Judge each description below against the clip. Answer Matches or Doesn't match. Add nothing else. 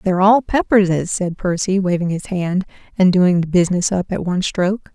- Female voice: Matches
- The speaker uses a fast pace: Doesn't match